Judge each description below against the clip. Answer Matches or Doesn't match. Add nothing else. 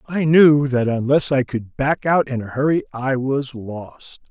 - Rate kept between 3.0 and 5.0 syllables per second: Matches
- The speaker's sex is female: Doesn't match